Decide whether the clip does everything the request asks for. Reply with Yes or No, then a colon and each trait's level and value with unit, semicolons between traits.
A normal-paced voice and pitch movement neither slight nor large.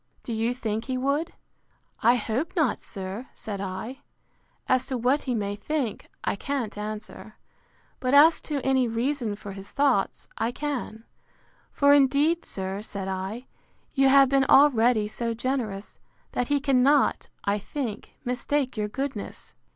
Yes: average, 150 wpm; average, 4.6 semitones